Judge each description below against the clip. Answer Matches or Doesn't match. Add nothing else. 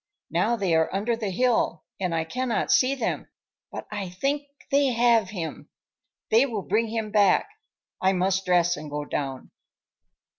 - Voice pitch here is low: Doesn't match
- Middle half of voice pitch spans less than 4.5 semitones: Doesn't match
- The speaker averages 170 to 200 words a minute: Doesn't match